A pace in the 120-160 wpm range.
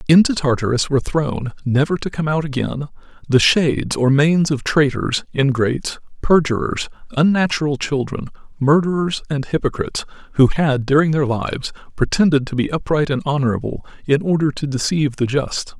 Yes: average, 150 wpm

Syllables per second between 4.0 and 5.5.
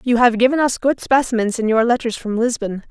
No: 5.7 syllables/s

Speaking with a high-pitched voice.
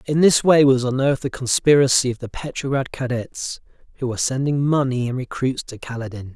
No: low, 130 Hz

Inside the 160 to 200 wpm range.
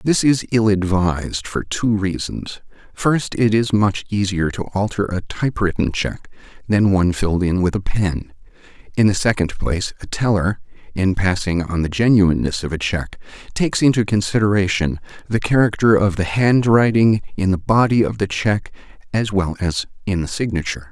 Yes: average, 165 wpm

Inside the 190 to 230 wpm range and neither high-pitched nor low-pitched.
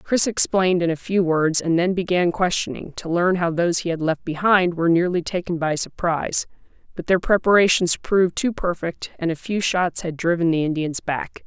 Yes: average, 200 wpm; medium, 175 Hz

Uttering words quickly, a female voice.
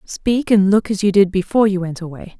Yes: fast, 250 wpm; female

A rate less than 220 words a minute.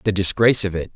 No: fast, 250 wpm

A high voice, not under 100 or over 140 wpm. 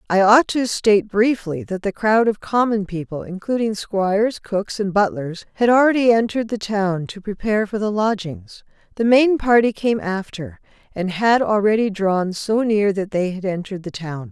No: high, 205 Hz; average, 180 wpm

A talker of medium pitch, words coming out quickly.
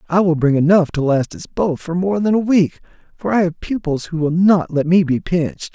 Yes: medium, 170 Hz; fast, 250 wpm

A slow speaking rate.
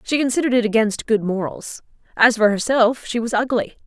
No: average, 185 wpm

